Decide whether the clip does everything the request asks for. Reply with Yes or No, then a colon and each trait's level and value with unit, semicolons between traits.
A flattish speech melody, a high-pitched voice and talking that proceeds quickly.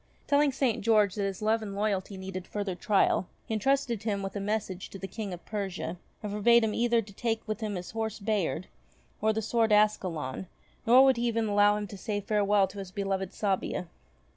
Yes: narrow, 2.2 semitones; high, 210 Hz; fast, 210 wpm